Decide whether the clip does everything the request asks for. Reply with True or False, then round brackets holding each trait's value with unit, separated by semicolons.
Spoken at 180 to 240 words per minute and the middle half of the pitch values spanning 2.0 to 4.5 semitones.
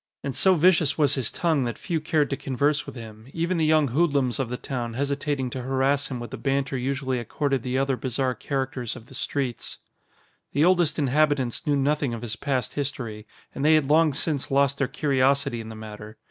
True (205 wpm; 2.8 semitones)